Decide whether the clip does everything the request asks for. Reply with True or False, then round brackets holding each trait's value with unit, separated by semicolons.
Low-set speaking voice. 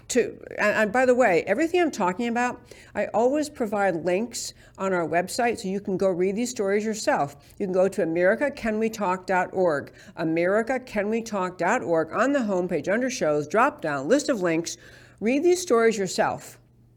False (205 Hz)